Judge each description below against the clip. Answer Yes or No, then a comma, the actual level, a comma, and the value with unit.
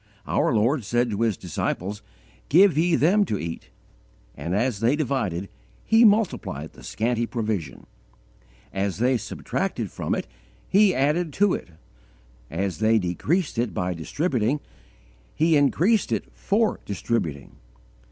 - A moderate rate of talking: No, slow, 130 wpm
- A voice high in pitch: No, low, 120 Hz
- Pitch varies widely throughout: Yes, wide, 8.3 semitones